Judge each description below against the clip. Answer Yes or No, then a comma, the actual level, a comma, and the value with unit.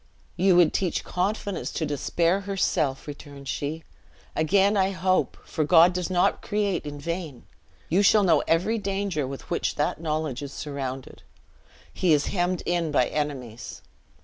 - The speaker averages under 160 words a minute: Yes, average, 150 wpm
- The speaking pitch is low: No, medium, 165 Hz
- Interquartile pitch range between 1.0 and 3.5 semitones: No, average, 4.4 semitones